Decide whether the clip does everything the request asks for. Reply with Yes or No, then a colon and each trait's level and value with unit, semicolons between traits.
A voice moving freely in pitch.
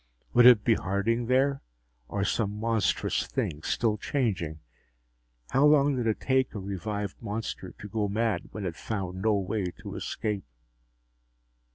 No: average, 3.2 semitones